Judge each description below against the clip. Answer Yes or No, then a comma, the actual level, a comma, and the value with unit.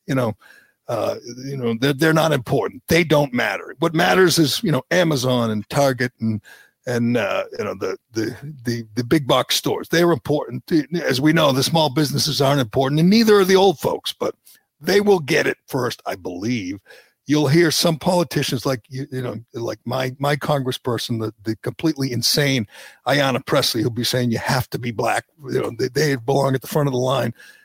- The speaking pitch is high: No, medium, 140 Hz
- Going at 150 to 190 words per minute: No, average, 200 wpm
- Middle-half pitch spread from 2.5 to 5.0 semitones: Yes, average, 4.3 semitones